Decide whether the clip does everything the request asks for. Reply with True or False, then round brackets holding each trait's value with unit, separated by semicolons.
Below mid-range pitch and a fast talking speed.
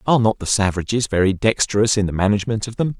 True (105 Hz; 220 wpm)